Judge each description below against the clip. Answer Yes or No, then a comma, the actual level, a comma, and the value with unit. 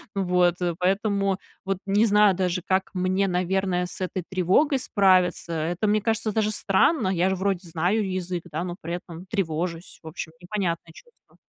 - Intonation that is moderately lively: No, narrow, 2.1 semitones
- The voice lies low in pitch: No, medium, 185 Hz